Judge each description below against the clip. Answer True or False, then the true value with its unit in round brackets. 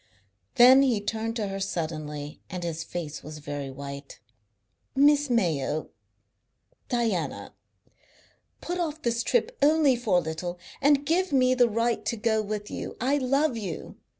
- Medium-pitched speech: False (225 Hz)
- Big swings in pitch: True (8.4 semitones)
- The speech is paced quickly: False (150 wpm)